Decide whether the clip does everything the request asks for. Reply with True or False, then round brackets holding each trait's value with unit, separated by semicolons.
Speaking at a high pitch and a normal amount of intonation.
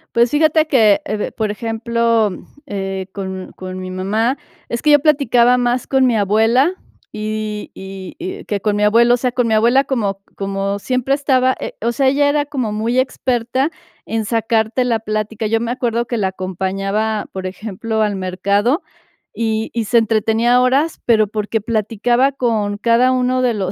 True (225 Hz; 3.3 semitones)